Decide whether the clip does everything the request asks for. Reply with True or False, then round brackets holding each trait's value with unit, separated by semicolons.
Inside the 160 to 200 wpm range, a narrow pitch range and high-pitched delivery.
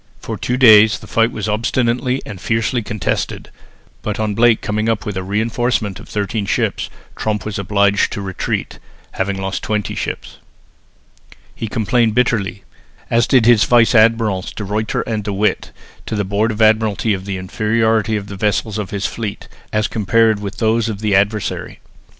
False (175 wpm; 1.9 semitones; 110 Hz)